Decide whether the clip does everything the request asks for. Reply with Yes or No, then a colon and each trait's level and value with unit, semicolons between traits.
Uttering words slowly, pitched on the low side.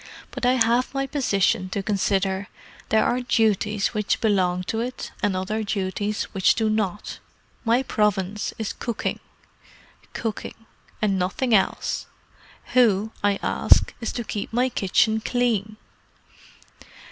No: slow, 130 wpm; high, 215 Hz